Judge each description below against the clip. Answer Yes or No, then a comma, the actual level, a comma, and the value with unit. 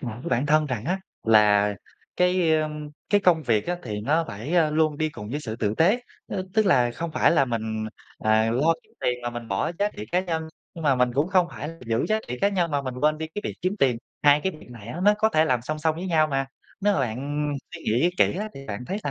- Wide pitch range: Yes, wide, 6.0 semitones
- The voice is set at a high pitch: No, medium, 150 Hz